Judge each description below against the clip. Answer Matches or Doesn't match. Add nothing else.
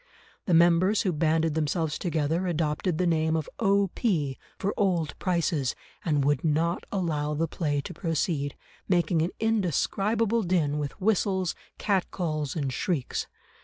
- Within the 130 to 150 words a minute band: Matches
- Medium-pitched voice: Matches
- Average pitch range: Matches